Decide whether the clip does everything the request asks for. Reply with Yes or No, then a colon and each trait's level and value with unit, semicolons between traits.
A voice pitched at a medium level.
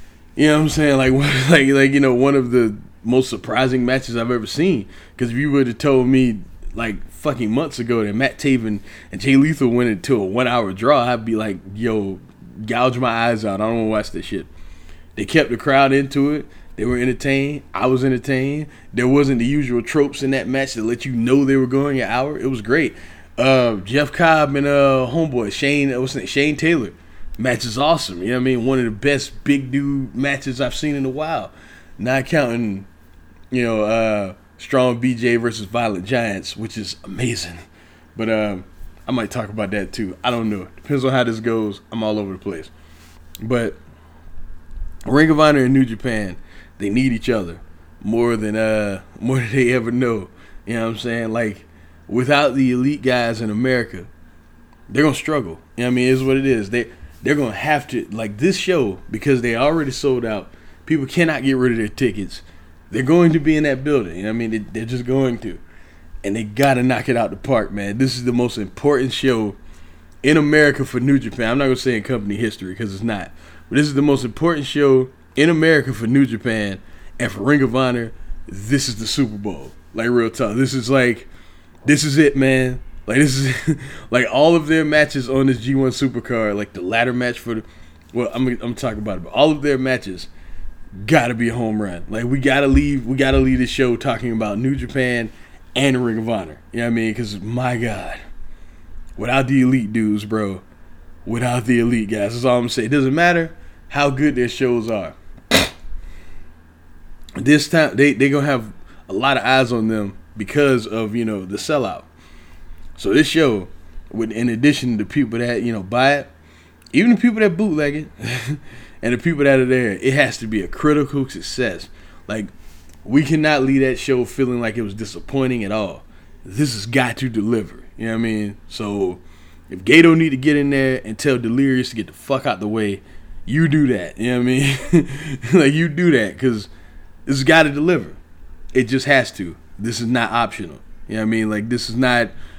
No: low, 120 Hz